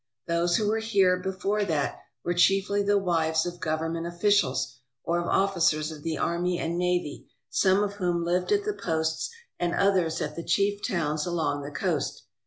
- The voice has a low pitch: No, medium, 175 Hz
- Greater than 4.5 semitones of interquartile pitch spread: No, average, 3.3 semitones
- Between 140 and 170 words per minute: No, average, 185 wpm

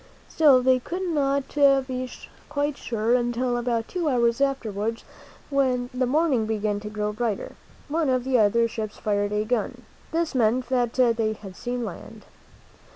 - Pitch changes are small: No, average, 3.2 semitones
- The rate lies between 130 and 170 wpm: Yes, average, 160 wpm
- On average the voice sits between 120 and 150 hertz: No, high, 245 Hz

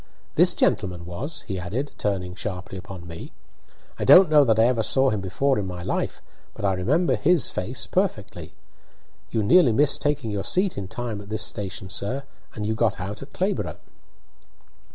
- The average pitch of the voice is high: No, low, 105 Hz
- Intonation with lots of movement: Yes, wide, 6.2 semitones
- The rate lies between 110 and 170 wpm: No, average, 180 wpm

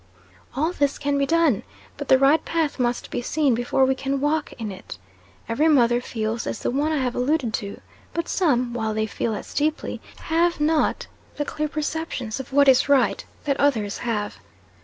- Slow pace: No, average, 190 wpm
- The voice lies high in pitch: Yes, very high, 275 Hz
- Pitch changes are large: No, average, 4.0 semitones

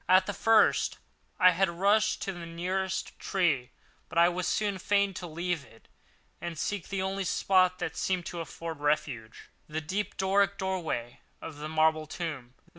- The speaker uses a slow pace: No, average, 170 wpm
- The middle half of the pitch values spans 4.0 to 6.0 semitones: No, average, 3.4 semitones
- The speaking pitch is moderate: Yes, medium, 175 Hz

